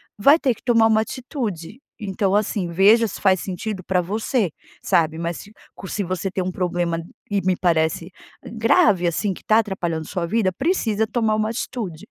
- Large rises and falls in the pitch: No, average, 4.0 semitones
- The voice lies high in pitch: Yes, high, 195 Hz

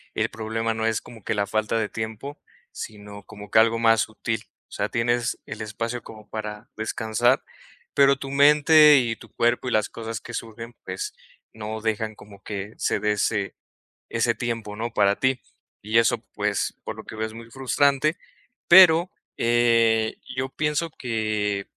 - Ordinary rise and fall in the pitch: No, narrow, 2.1 semitones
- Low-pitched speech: Yes, low, 115 Hz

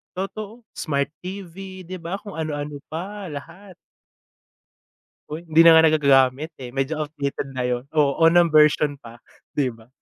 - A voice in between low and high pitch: Yes, medium, 155 Hz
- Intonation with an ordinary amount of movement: Yes, average, 4.3 semitones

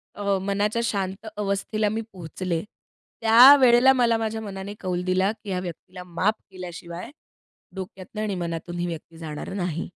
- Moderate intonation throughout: Yes, average, 3.4 semitones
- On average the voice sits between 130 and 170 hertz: No, high, 190 Hz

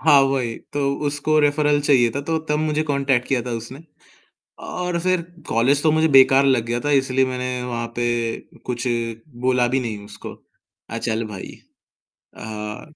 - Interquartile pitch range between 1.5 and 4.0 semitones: Yes, average, 3.5 semitones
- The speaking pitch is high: No, low, 130 Hz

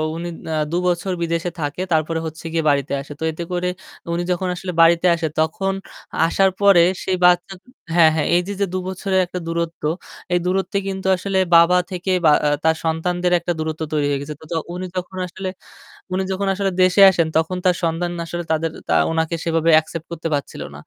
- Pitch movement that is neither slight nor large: No, narrow, 2.2 semitones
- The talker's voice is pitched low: No, medium, 175 Hz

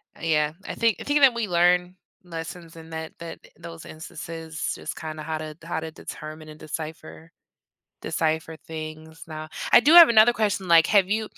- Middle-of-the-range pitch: Yes, medium, 165 Hz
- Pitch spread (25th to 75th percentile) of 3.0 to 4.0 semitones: No, narrow, 2.6 semitones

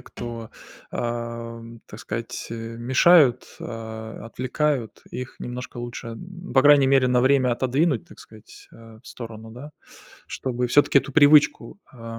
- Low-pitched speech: Yes, low, 120 Hz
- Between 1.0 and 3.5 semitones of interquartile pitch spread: Yes, average, 2.7 semitones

